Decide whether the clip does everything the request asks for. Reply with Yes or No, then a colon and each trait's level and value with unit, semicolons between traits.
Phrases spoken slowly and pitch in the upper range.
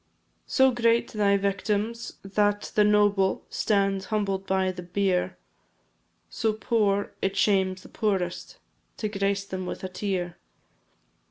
Yes: slow, 125 wpm; high, 200 Hz